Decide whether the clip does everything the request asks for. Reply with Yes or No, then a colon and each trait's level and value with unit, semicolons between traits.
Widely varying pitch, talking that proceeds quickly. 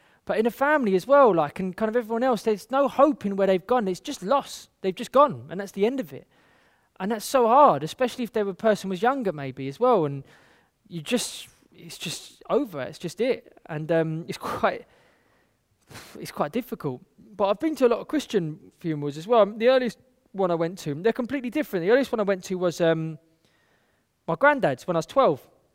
Yes: wide, 6.9 semitones; fast, 220 wpm